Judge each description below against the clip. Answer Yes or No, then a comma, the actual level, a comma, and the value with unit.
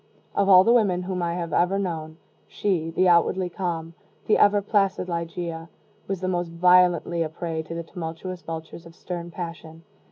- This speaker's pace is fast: No, average, 180 wpm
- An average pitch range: No, narrow, 1.9 semitones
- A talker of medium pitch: Yes, medium, 175 Hz